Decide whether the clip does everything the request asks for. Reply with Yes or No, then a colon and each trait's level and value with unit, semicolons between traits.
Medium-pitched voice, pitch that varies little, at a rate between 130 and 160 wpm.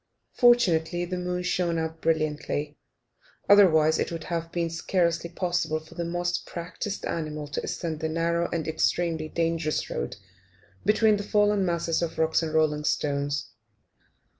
Yes: medium, 165 Hz; narrow, 1.8 semitones; average, 145 wpm